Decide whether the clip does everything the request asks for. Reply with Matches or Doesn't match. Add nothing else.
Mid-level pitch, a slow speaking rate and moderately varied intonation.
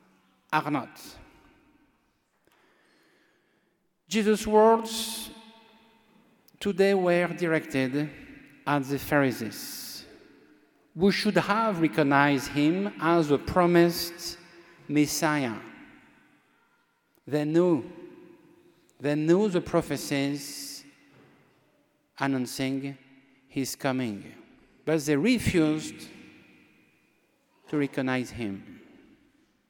Doesn't match